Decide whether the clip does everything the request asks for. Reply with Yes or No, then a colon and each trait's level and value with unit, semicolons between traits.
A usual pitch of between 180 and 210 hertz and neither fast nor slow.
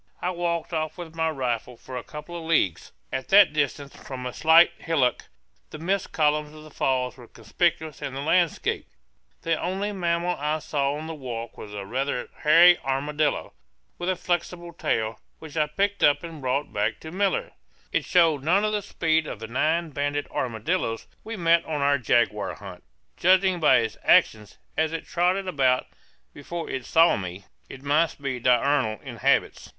No: medium, 150 Hz; average, 180 wpm